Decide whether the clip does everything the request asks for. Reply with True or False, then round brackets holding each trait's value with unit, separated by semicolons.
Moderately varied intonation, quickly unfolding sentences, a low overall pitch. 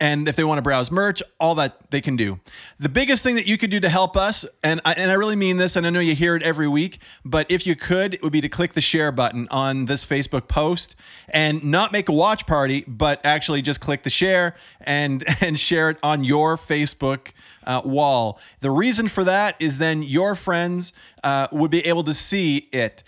False (3.8 semitones; 230 wpm; 155 Hz)